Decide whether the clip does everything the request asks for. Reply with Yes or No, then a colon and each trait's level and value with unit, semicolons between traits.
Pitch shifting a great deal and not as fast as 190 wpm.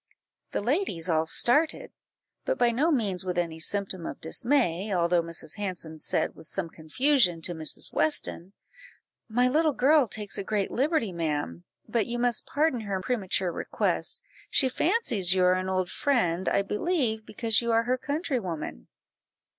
Yes: wide, 6.4 semitones; average, 160 wpm